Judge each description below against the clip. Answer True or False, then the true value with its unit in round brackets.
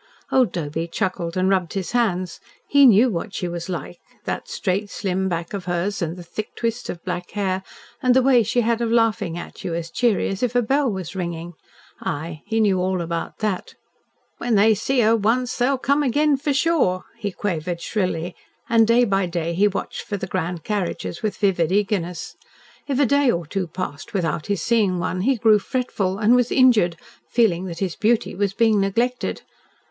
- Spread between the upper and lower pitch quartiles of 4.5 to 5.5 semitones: True (4.8 semitones)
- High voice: True (200 Hz)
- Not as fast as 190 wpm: False (195 wpm)